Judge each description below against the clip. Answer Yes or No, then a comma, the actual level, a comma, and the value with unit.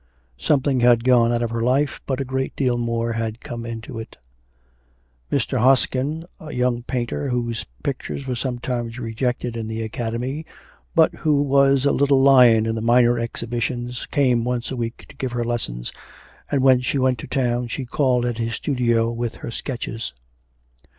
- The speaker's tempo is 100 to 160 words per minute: No, average, 175 wpm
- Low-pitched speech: Yes, low, 120 Hz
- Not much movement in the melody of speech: Yes, narrow, 2.2 semitones